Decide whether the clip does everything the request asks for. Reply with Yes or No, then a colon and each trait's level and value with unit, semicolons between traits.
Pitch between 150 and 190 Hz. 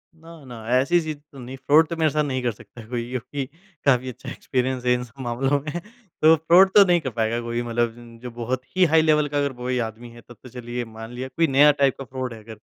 No: low, 130 Hz